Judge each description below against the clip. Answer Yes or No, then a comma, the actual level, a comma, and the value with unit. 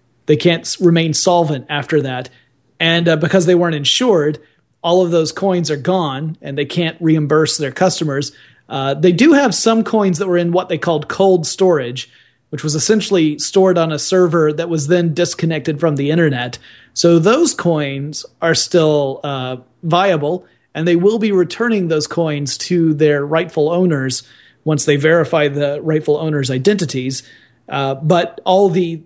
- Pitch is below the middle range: No, medium, 160 Hz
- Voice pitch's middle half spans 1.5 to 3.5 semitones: Yes, average, 3.2 semitones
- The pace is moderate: Yes, average, 165 wpm